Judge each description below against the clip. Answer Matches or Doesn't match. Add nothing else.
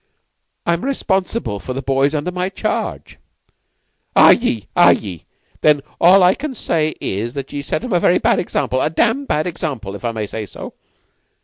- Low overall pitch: Doesn't match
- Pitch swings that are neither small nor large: Doesn't match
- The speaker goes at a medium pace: Matches